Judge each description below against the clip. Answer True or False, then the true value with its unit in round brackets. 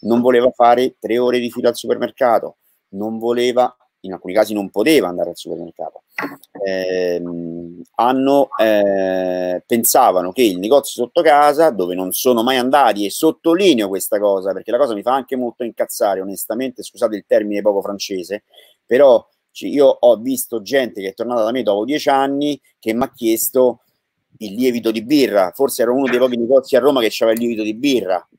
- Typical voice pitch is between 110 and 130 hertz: True (120 Hz)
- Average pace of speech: False (185 wpm)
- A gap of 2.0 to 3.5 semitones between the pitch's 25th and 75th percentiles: False (4.6 semitones)